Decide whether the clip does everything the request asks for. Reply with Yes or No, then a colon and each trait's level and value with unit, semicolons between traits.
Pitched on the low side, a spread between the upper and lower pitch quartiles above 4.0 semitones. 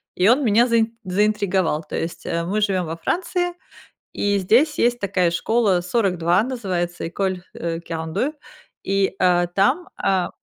No: high, 195 Hz; average, 4.7 semitones